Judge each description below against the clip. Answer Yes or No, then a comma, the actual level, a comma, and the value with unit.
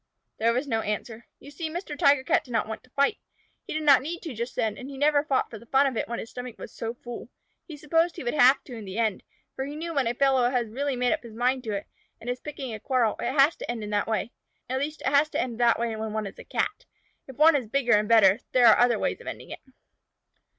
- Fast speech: Yes, fast, 285 wpm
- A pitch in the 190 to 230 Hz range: No, very high, 250 Hz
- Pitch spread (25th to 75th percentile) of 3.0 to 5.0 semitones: Yes, average, 3.8 semitones